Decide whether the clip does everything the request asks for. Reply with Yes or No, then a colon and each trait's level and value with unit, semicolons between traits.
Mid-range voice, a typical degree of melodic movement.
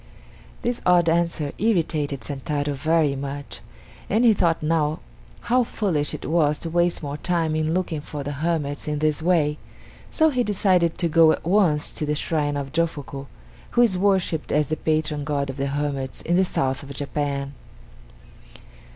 Yes: medium, 155 Hz; average, 3.1 semitones